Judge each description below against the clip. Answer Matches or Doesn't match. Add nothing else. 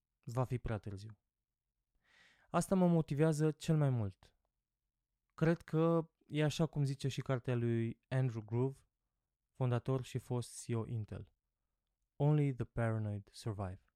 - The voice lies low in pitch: Matches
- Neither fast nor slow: Matches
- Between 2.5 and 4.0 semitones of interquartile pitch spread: Doesn't match